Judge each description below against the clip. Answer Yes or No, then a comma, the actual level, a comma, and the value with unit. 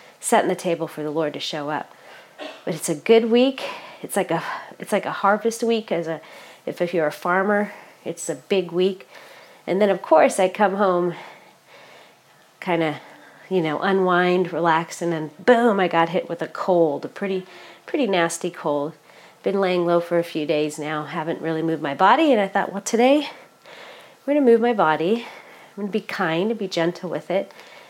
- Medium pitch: Yes, medium, 180 Hz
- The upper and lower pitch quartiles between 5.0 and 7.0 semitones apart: No, average, 3.9 semitones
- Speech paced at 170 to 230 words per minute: Yes, average, 200 wpm